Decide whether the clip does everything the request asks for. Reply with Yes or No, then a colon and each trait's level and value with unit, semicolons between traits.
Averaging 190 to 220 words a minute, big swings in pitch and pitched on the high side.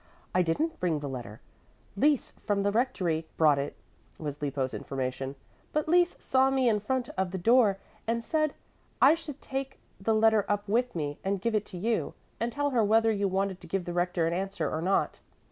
Yes: fast, 205 wpm; wide, 6.3 semitones; high, 200 Hz